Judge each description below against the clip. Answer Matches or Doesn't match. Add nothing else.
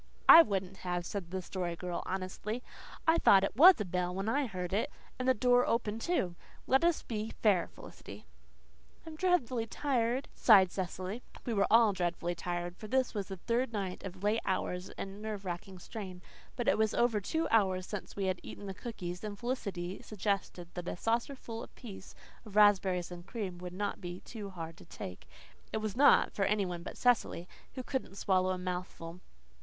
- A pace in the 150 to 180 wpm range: Doesn't match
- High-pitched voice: Matches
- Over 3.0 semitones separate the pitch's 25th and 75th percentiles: Matches